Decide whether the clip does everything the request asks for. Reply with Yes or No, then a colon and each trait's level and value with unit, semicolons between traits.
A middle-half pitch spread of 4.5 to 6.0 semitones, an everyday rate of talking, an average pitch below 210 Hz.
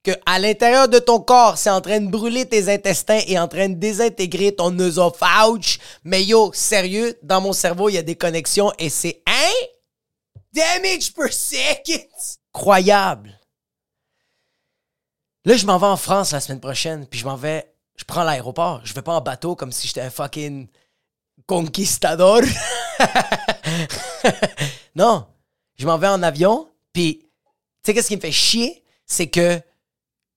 Yes: average, 5.2 semitones; average, 160 wpm; high, 190 Hz